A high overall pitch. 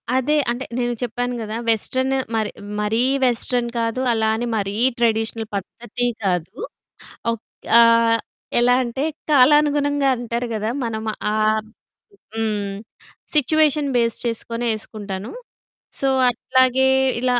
Yes: high, 235 Hz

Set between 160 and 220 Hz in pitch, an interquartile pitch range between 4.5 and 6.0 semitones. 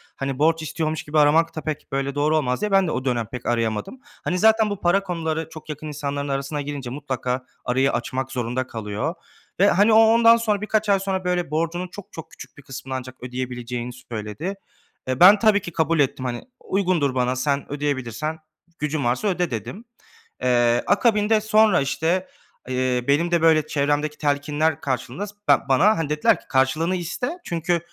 No: medium, 150 Hz; wide, 5.6 semitones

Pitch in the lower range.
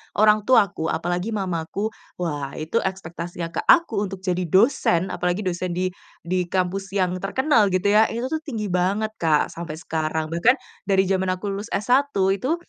No: high, 190 Hz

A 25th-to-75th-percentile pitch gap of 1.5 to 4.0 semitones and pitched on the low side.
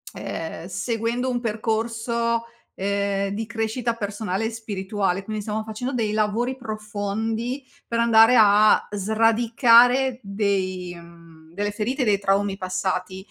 No: average, 2.8 semitones; high, 215 Hz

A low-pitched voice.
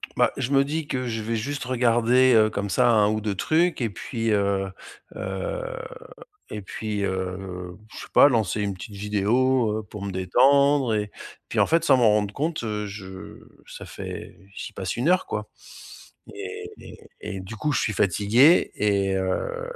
Yes: low, 110 Hz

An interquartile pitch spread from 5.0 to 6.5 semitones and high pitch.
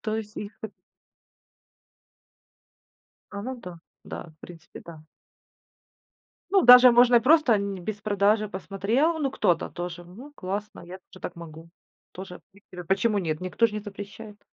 No: average, 4.1 semitones; high, 200 Hz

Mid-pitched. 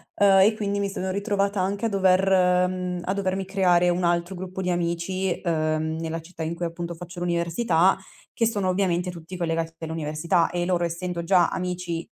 Yes: medium, 180 Hz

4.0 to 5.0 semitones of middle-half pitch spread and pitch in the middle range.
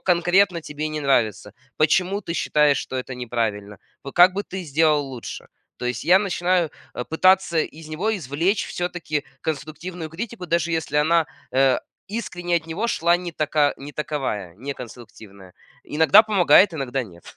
Yes: average, 4.6 semitones; medium, 155 Hz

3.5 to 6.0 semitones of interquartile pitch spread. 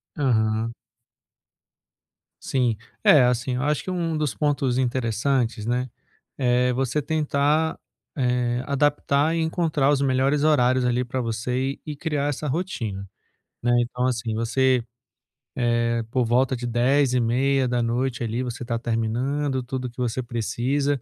No: average, 2.9 semitones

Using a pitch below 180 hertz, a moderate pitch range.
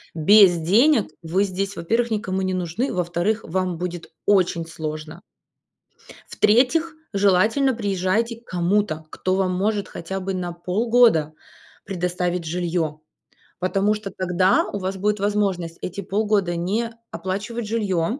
No: high, 190 Hz; average, 3.2 semitones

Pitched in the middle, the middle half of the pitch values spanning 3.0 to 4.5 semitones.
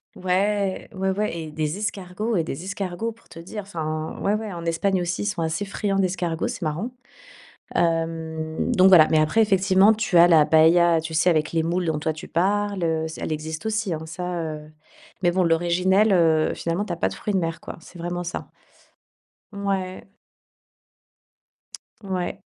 Yes: medium, 175 Hz; average, 3.3 semitones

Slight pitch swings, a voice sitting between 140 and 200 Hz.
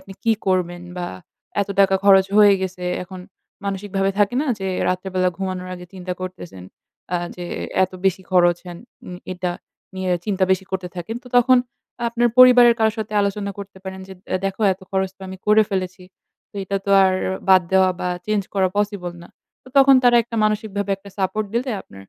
Yes: narrow, 2.1 semitones; high, 190 Hz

